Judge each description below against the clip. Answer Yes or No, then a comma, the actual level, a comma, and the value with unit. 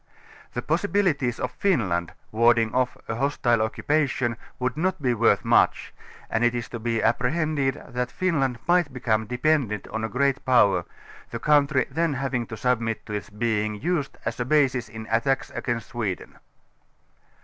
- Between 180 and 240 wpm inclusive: No, average, 160 wpm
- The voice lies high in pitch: No, low, 125 Hz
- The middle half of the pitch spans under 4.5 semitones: Yes, average, 3.9 semitones